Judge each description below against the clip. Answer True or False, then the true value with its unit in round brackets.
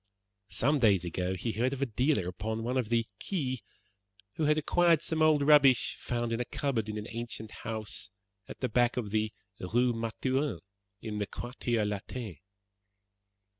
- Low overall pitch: True (120 Hz)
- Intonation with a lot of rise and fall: False (3.7 semitones)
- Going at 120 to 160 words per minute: False (170 wpm)